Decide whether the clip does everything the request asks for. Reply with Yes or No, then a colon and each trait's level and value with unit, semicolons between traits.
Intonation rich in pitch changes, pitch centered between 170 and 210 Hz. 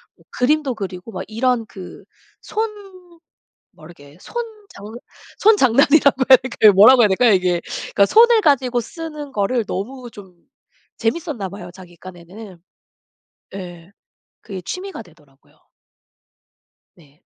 No: wide, 7.6 semitones; high, 225 Hz